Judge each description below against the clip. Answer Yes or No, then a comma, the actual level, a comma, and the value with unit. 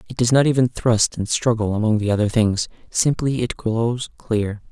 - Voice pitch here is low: Yes, low, 115 Hz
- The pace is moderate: Yes, average, 190 wpm